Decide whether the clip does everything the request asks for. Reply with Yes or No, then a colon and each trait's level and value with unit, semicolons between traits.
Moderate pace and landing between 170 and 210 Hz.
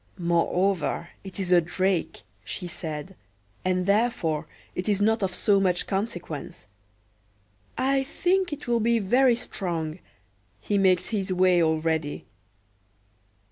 No: slow, 125 wpm; medium, 185 Hz